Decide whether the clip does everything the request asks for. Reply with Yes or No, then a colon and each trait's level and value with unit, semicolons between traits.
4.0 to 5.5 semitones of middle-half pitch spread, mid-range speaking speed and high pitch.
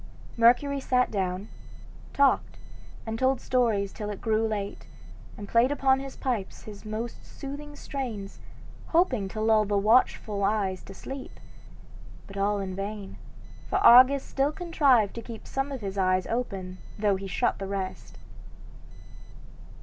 Yes: average, 4.7 semitones; average, 145 wpm; high, 220 Hz